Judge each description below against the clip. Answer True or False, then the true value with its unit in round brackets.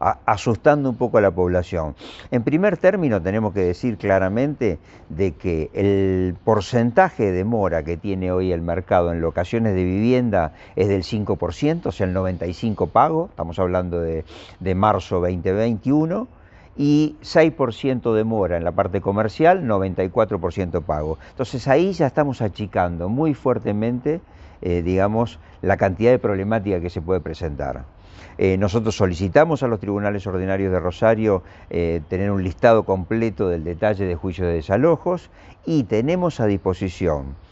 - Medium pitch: False (100 Hz)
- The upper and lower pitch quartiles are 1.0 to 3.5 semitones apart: False (4.7 semitones)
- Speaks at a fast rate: False (150 wpm)